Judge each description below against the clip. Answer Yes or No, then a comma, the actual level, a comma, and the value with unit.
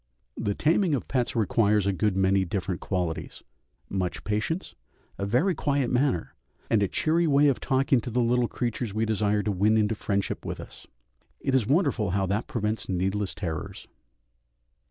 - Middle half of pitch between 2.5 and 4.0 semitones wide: No, average, 4.7 semitones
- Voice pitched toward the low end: Yes, low, 110 Hz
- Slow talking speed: No, average, 170 wpm